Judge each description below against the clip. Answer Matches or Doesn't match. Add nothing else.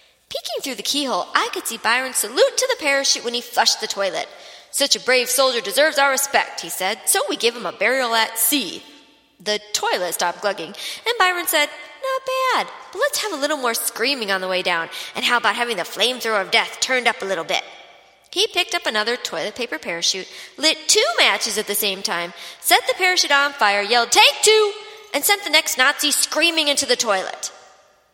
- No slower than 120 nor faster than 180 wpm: Doesn't match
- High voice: Matches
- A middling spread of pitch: Doesn't match